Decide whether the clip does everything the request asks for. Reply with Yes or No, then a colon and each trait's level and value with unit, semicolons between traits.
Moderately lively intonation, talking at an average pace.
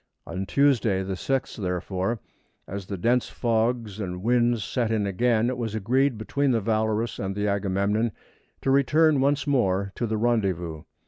Yes: average, 3.9 semitones; average, 155 wpm